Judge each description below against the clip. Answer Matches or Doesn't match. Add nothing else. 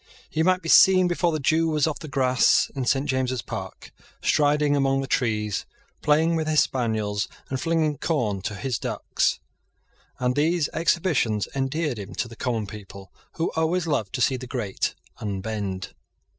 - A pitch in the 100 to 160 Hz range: Matches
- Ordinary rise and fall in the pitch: Doesn't match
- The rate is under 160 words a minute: Doesn't match